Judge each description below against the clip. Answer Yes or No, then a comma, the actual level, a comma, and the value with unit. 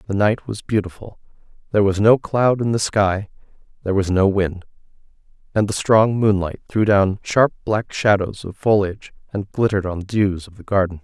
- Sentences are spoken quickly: No, average, 185 wpm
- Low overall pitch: Yes, low, 100 Hz